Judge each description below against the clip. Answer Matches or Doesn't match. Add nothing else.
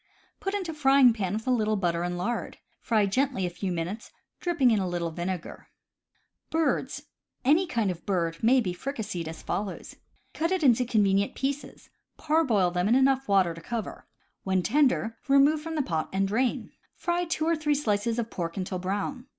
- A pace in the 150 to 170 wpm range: Doesn't match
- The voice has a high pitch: Matches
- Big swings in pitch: Matches